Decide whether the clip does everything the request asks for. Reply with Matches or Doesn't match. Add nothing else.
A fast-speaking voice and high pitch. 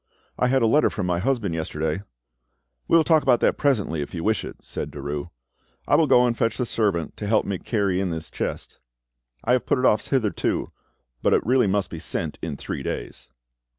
Doesn't match